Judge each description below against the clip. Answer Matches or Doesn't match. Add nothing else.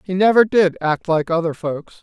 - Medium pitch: Matches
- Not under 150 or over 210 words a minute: Matches